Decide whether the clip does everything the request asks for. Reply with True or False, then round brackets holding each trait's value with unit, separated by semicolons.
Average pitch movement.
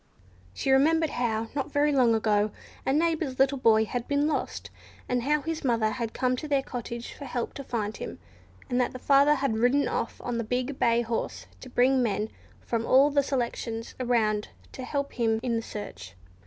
True (3.6 semitones)